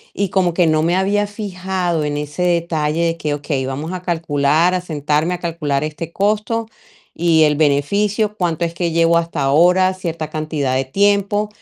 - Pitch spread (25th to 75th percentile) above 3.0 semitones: Yes, average, 3.5 semitones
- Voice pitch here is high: No, medium, 170 Hz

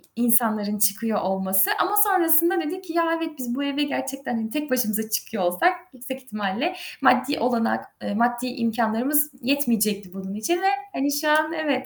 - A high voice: Yes, very high, 250 Hz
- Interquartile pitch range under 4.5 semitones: No, wide, 5.6 semitones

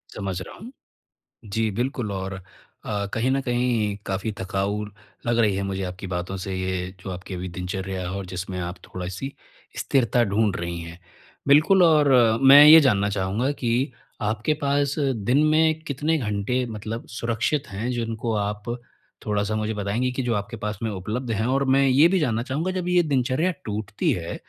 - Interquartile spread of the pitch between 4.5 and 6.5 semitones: Yes, average, 5.1 semitones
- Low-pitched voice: Yes, low, 110 Hz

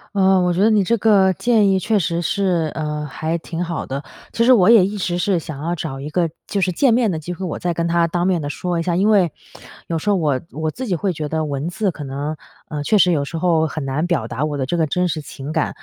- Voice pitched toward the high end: No, medium, 170 Hz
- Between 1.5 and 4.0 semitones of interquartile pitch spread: Yes, average, 3.6 semitones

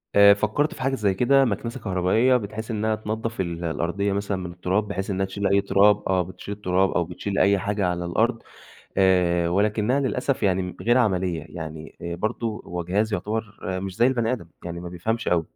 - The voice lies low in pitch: Yes, low, 100 Hz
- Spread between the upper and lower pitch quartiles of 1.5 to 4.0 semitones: Yes, average, 3.4 semitones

